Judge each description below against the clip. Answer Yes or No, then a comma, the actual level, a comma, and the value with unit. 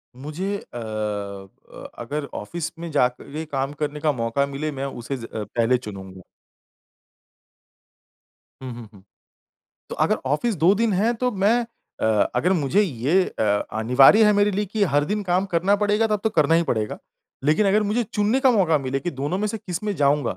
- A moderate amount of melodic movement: No, wide, 7.9 semitones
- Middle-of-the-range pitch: Yes, medium, 155 Hz